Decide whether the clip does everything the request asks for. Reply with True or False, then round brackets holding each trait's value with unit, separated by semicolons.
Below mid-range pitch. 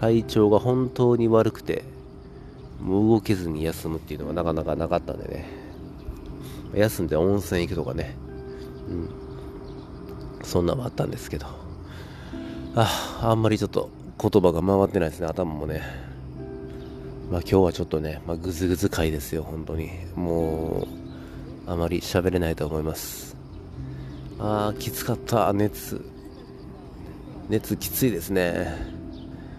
True (80 Hz)